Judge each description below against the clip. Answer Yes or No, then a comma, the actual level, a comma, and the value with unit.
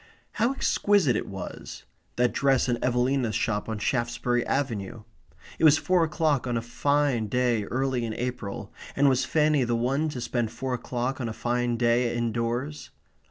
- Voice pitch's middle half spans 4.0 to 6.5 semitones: No, average, 2.7 semitones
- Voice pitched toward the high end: No, low, 125 Hz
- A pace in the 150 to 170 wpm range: Yes, average, 165 wpm